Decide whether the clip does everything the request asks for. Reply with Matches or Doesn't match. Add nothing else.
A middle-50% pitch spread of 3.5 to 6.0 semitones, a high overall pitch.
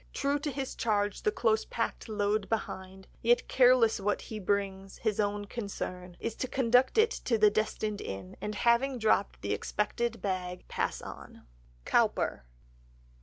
Doesn't match